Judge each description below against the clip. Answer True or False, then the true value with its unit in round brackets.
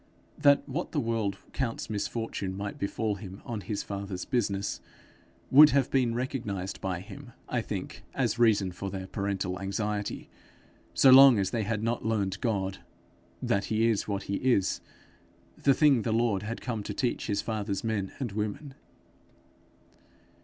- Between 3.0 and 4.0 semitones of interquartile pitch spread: True (3.3 semitones)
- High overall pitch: False (105 Hz)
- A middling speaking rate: True (160 wpm)